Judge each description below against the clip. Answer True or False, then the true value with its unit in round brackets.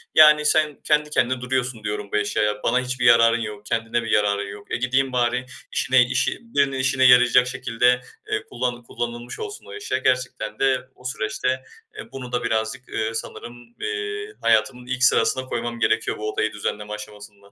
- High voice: False (125 Hz)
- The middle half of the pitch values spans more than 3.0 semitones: False (2.7 semitones)